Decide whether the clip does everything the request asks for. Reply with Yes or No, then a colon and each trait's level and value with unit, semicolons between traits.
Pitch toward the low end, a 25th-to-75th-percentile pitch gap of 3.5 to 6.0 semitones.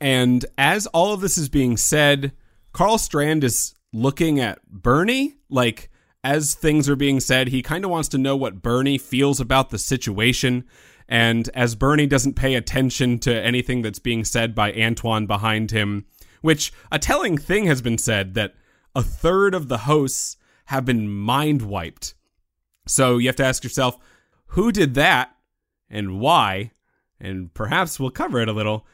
Yes: low, 125 Hz; average, 4.3 semitones